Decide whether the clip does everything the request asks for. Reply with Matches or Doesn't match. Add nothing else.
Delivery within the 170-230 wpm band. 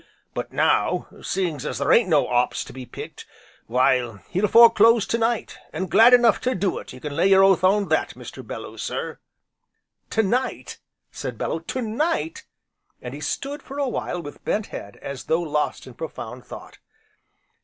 Matches